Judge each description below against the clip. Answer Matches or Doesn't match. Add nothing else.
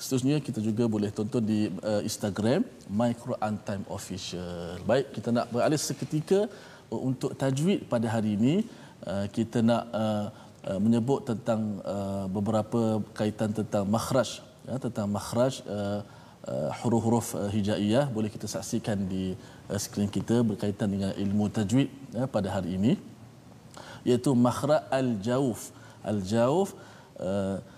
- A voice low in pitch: Matches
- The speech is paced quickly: Matches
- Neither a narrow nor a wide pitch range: Matches